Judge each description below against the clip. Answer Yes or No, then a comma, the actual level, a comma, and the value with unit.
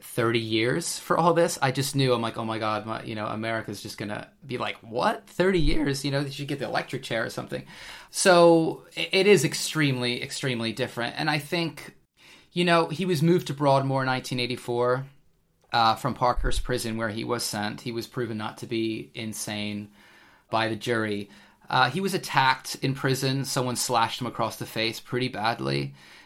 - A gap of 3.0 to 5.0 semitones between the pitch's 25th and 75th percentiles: Yes, average, 4.5 semitones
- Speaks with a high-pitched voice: No, low, 125 Hz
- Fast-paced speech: No, average, 190 wpm